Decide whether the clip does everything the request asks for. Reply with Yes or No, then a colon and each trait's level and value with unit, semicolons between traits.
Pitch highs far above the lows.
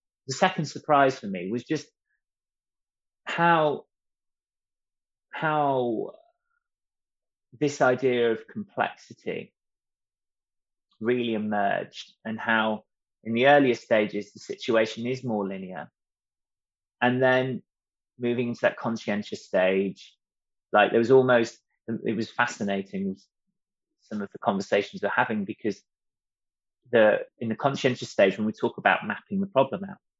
Yes: wide, 5.7 semitones